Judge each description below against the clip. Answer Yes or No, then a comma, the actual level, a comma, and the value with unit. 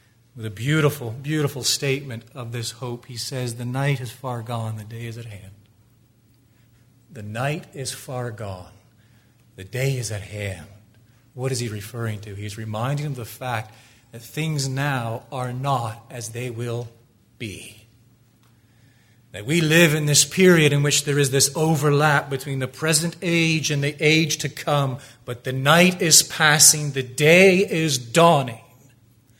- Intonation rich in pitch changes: No, average, 3.8 semitones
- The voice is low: Yes, low, 125 Hz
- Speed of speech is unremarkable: Yes, average, 165 wpm